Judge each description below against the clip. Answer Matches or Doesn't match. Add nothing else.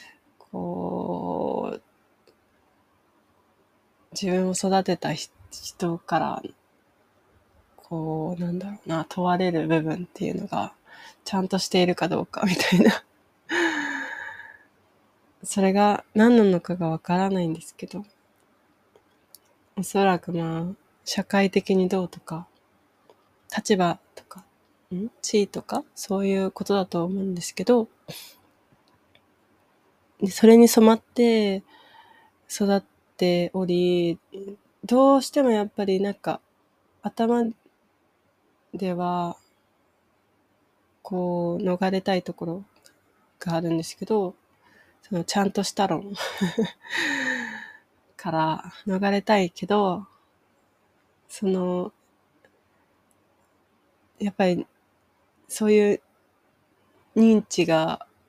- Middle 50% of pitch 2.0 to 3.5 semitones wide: Matches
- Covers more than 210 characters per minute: Doesn't match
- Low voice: Doesn't match